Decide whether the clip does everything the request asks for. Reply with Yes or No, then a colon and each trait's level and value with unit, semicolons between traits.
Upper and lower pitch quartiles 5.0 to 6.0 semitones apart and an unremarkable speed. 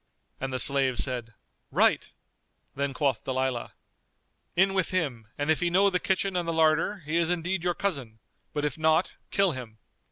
Yes: average, 5.3 semitones; average, 180 wpm